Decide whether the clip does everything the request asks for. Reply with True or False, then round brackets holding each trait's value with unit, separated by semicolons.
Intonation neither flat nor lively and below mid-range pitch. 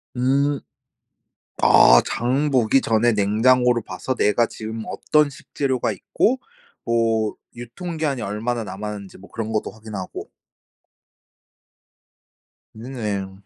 True (3.3 semitones; 115 Hz)